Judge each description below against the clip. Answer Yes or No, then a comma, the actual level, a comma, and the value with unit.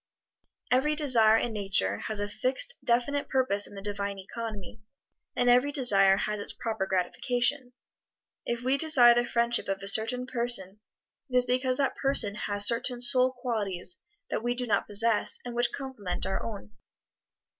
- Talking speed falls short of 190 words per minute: Yes, average, 165 wpm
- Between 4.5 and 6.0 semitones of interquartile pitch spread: No, average, 3.8 semitones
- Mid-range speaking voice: No, high, 235 Hz